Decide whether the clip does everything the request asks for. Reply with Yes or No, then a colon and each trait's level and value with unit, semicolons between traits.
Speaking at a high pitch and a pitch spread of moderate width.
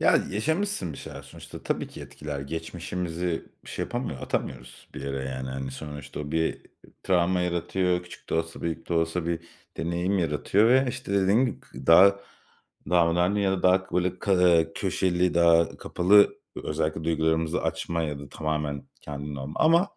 No: very low, 85 Hz; average, 3.3 semitones